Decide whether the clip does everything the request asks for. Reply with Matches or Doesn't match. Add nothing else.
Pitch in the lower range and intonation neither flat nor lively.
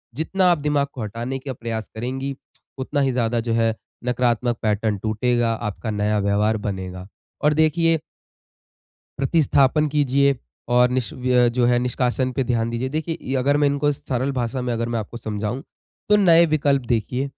Matches